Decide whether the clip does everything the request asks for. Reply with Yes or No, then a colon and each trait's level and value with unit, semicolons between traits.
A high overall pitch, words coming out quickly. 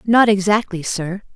No: high, 200 Hz; slow, 135 wpm